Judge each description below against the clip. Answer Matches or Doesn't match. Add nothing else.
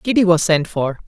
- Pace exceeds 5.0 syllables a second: Matches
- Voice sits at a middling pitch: Matches